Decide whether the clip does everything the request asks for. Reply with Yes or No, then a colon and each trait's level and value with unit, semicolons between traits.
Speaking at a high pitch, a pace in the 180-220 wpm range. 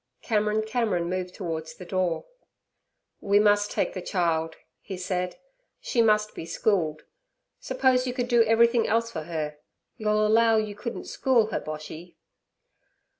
No: high, 205 Hz; average, 145 wpm